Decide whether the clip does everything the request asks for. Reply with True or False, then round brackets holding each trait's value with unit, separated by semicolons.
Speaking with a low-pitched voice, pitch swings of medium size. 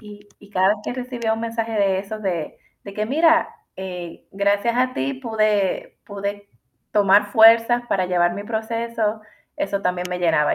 False (205 Hz; 3.1 semitones)